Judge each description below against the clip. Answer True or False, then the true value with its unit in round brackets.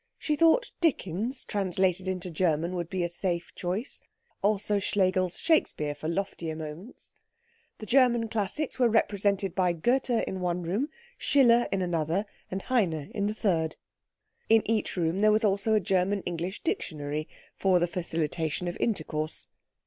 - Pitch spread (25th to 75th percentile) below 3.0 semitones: False (4.2 semitones)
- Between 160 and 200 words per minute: False (150 wpm)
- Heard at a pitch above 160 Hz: True (190 Hz)